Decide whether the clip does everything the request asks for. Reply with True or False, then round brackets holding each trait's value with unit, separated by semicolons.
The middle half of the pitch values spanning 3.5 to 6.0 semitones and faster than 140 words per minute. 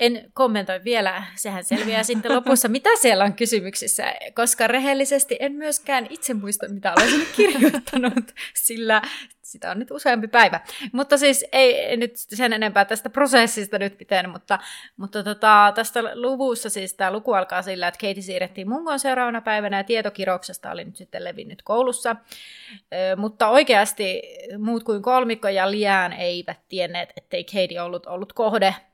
True (4.7 semitones; 150 wpm)